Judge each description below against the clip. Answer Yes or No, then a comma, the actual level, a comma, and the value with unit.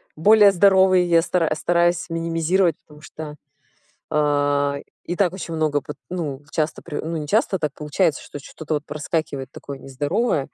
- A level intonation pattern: No, average, 3.1 semitones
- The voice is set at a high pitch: No, medium, 160 Hz